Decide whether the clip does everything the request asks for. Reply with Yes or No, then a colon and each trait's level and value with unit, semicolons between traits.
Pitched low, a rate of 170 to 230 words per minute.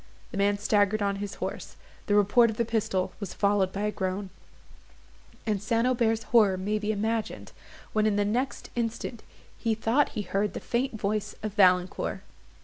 No: high, 210 Hz; average, 175 wpm